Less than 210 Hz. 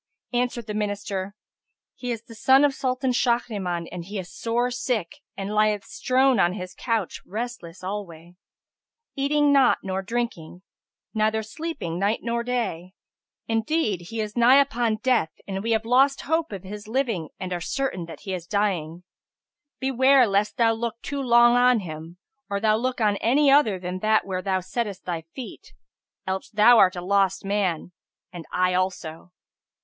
No: high, 215 Hz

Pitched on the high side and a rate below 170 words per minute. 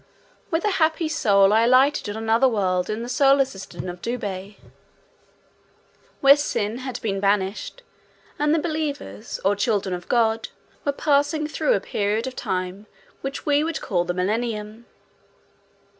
Yes: high, 230 Hz; average, 150 wpm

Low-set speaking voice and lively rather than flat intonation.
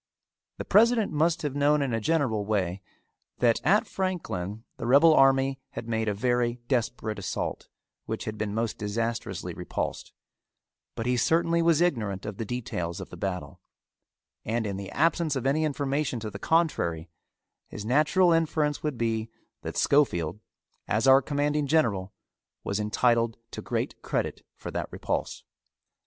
Yes: low, 125 Hz; wide, 5.9 semitones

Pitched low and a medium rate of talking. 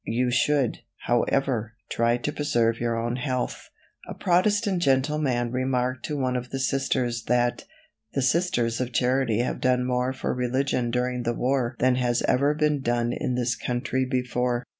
Yes: low, 125 Hz; average, 160 wpm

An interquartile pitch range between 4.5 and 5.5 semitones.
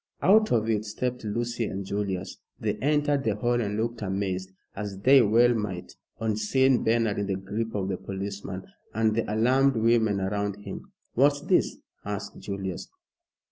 No: average, 3.1 semitones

